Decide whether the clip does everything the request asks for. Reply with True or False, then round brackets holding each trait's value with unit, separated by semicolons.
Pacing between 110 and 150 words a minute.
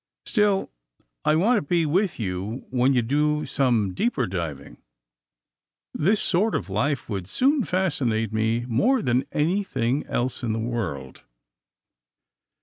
True (145 wpm)